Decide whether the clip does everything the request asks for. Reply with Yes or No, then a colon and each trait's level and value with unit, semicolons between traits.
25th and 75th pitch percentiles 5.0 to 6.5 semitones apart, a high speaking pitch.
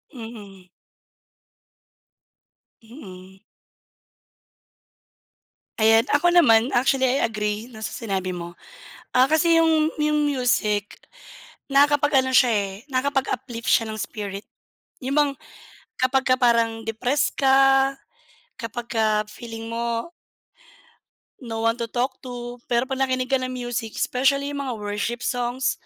No: average, 3.2 semitones; high, 240 Hz